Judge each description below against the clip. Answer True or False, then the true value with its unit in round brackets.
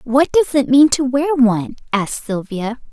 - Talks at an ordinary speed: True (185 wpm)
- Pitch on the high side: True (255 Hz)